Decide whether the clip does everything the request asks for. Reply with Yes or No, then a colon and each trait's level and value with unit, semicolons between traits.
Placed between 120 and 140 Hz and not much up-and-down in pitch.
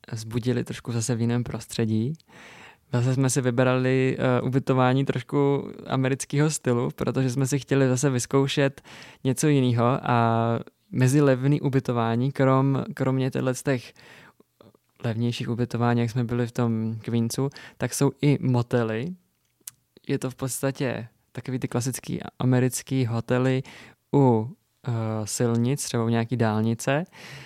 Yes: low, 130 Hz; narrow, 2.2 semitones